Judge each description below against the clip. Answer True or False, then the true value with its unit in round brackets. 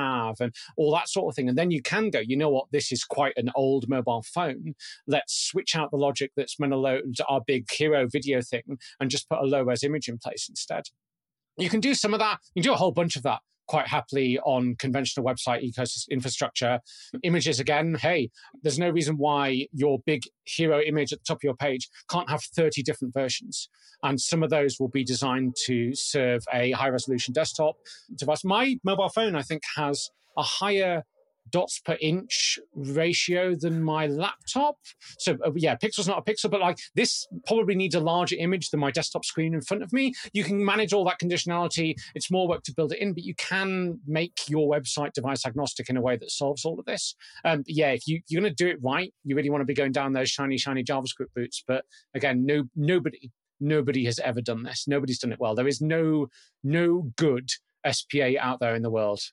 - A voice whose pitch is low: False (150 Hz)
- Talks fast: True (220 wpm)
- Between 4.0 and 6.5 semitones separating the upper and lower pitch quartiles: True (4.6 semitones)